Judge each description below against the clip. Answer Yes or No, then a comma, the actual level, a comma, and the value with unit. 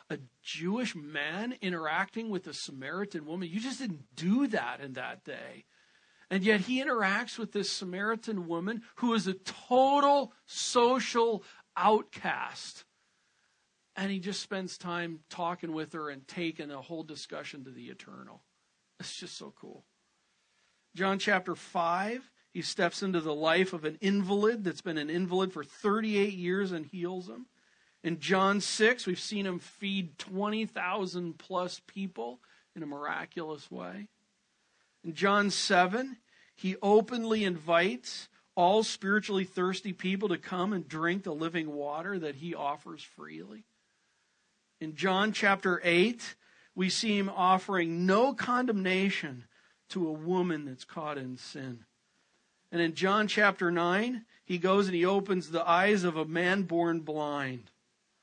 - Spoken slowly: No, average, 145 wpm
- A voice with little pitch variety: No, average, 3.7 semitones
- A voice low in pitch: No, medium, 185 Hz